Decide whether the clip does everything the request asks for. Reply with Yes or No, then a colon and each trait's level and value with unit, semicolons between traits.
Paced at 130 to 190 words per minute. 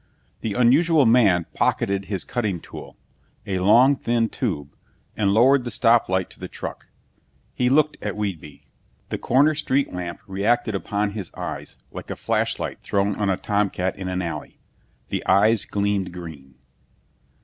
Yes: average, 155 wpm